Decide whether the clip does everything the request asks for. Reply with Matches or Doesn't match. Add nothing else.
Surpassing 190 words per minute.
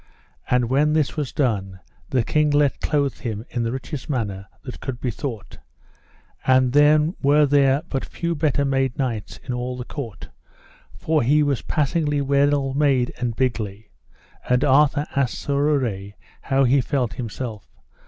Doesn't match